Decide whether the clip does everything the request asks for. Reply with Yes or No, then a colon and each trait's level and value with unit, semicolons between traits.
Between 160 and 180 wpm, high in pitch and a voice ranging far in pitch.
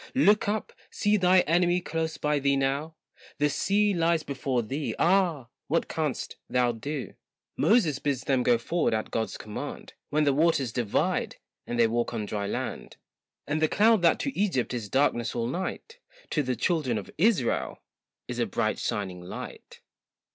No: average, 170 wpm; medium, 145 Hz; wide, 6.3 semitones